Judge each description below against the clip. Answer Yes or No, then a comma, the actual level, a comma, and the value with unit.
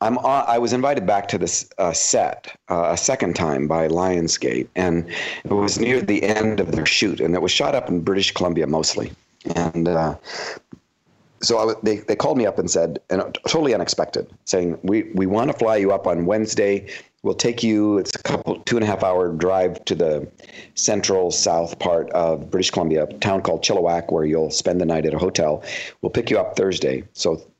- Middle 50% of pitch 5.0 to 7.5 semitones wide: No, average, 4.0 semitones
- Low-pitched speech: Yes, very low, 90 Hz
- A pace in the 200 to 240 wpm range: Yes, fast, 205 wpm